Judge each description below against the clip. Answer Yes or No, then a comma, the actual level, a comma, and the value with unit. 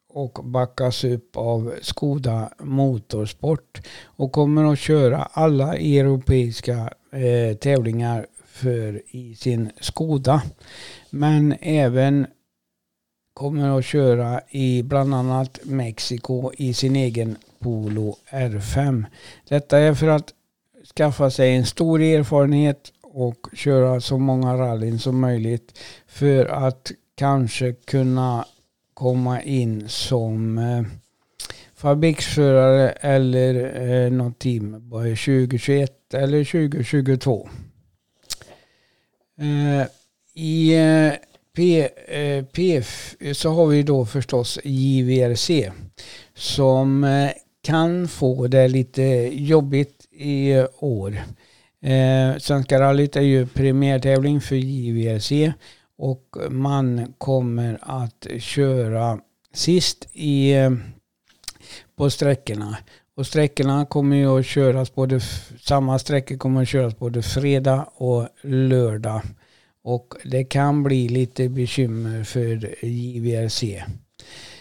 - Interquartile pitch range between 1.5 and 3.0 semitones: Yes, narrow, 2.6 semitones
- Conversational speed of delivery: No, slow, 95 wpm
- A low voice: Yes, low, 130 Hz